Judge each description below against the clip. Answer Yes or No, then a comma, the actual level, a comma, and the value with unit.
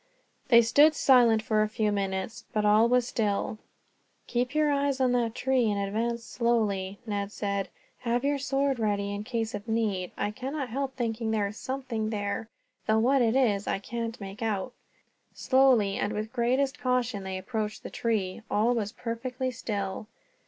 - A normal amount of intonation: Yes, average, 3.4 semitones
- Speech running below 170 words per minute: No, average, 175 wpm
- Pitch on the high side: Yes, high, 225 Hz